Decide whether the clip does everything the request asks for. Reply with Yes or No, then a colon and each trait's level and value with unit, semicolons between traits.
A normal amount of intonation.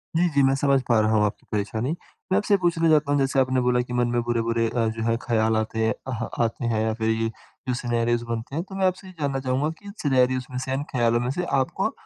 Yes: average, 3.5 semitones